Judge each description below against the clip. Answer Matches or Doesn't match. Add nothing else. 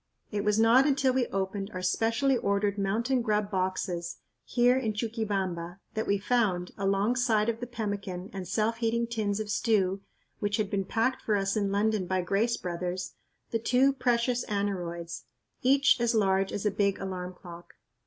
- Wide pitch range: Doesn't match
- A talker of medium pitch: Doesn't match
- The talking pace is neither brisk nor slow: Matches